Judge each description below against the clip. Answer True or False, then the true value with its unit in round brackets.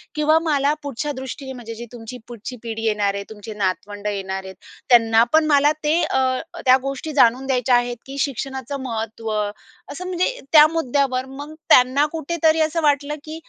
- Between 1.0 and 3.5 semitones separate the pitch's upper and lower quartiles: False (4.6 semitones)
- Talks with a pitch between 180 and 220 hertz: False (265 Hz)